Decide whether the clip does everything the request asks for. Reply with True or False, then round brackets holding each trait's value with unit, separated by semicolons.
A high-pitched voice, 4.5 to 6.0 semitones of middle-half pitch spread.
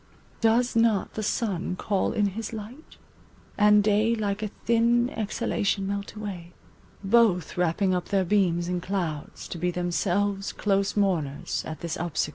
False (200 Hz; 3.2 semitones)